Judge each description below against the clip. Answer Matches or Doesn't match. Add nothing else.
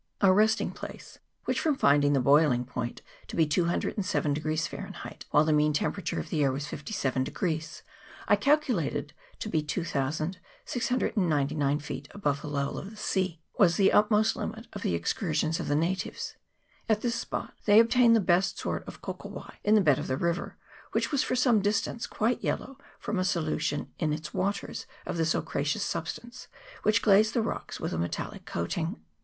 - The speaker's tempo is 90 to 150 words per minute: Doesn't match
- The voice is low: Doesn't match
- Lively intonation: Matches